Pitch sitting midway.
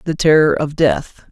Yes: medium, 150 Hz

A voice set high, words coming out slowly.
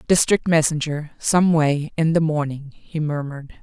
No: medium, 155 Hz; slow, 115 wpm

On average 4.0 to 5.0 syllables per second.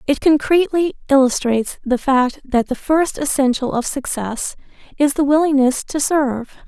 Yes: 4.9 syllables/s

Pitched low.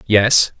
Yes: low, 110 Hz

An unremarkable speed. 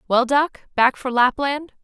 Yes: average, 165 wpm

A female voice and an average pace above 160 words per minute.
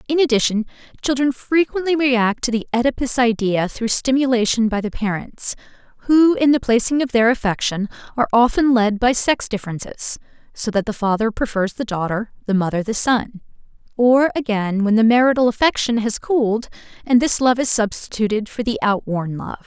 Yes: female; average, 170 wpm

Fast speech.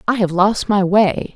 Yes: fast, 220 wpm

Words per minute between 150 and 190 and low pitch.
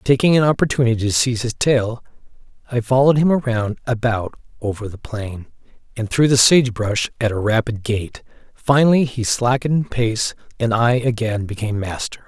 Yes: average, 160 wpm; low, 120 Hz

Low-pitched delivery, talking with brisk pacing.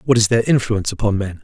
Yes: low, 110 Hz; fast, 250 wpm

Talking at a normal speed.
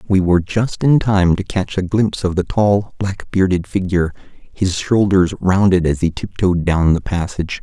Yes: average, 190 wpm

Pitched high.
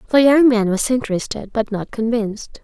Yes: high, 225 Hz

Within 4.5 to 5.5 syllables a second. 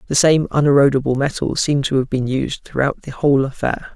No: 5.9 syllables/s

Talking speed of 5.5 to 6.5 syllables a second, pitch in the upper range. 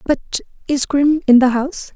No: 4.7 syllables/s; very high, 275 Hz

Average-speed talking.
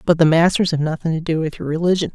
No: fast, 280 wpm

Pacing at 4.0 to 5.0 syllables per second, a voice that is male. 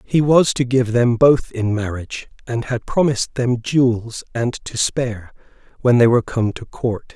Yes: 4.6 syllables/s; male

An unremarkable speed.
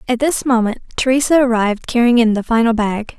Yes: average, 190 wpm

